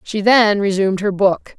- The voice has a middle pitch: No, high, 200 Hz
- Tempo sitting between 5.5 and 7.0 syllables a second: No, 4.7 syllables/s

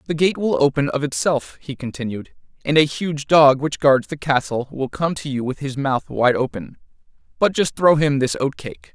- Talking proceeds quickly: Yes, fast, 215 wpm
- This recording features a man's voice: Yes, male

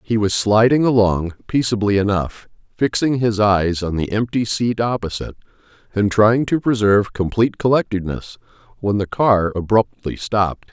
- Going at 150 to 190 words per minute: No, average, 140 wpm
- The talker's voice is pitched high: No, low, 105 Hz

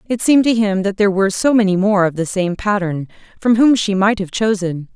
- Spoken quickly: Yes, fast, 240 wpm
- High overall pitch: Yes, high, 200 Hz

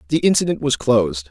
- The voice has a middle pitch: Yes, medium, 150 Hz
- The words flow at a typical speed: Yes, average, 185 wpm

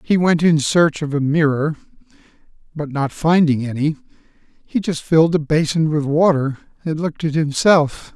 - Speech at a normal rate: Yes, average, 160 wpm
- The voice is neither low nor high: Yes, medium, 155 Hz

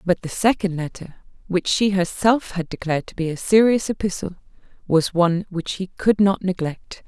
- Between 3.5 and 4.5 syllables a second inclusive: No, 5.1 syllables/s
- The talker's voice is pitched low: No, medium, 185 Hz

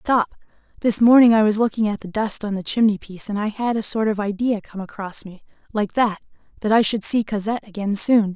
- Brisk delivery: Yes, fast, 230 wpm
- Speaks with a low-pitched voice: No, high, 210 Hz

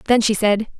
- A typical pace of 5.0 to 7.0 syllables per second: Yes, 5.5 syllables/s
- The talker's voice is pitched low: No, high, 215 Hz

